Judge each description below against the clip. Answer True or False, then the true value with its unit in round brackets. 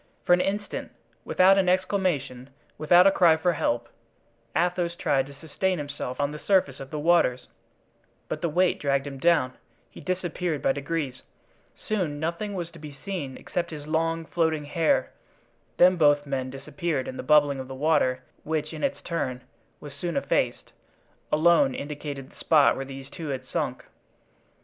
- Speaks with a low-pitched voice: False (155 Hz)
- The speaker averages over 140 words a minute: True (170 wpm)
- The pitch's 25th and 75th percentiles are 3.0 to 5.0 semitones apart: True (3.9 semitones)